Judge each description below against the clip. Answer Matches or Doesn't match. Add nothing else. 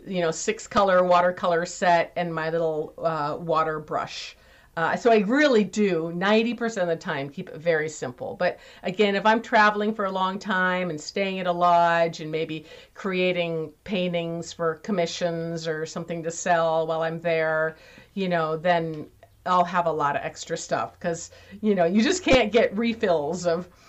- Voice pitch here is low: Doesn't match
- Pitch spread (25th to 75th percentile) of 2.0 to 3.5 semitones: Matches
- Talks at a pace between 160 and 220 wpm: Matches